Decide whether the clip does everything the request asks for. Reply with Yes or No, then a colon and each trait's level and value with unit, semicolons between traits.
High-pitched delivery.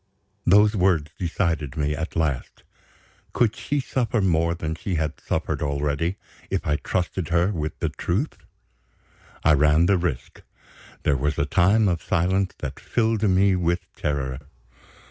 No: very low, 85 Hz